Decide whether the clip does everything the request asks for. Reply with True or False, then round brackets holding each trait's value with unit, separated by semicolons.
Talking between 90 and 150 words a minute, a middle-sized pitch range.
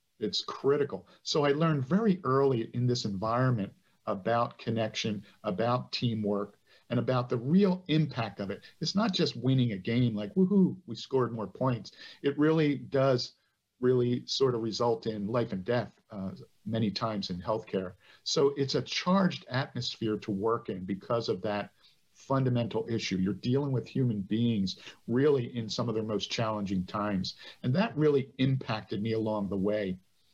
False (165 wpm; 3.9 semitones)